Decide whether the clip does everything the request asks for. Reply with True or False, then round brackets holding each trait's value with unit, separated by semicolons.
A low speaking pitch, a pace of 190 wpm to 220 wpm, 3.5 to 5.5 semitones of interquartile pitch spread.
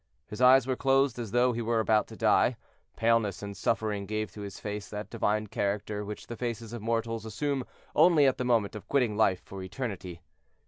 False (110 Hz; 200 wpm; 2.9 semitones)